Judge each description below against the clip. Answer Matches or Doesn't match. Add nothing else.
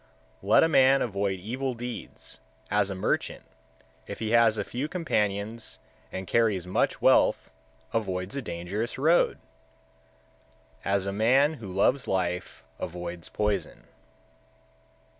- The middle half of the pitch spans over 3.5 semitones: Matches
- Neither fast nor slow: Doesn't match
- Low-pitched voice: Matches